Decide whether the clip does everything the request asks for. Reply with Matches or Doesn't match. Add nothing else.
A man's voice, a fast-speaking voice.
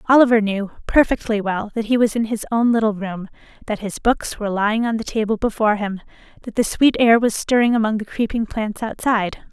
Doesn't match